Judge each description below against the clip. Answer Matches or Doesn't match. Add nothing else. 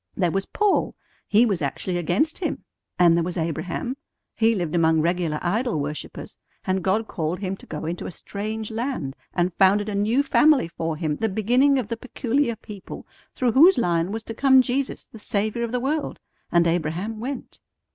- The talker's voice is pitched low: Doesn't match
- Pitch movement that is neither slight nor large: Doesn't match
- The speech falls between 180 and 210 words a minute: Matches